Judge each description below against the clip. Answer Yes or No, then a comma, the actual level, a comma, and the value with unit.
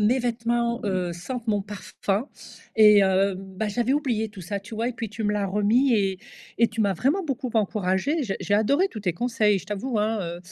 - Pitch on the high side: Yes, high, 215 Hz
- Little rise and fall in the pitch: No, average, 3.2 semitones